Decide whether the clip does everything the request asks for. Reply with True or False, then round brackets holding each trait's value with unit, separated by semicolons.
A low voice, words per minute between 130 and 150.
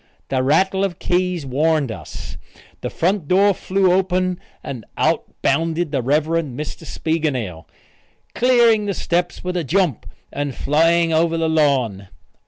False (165 Hz; 140 wpm)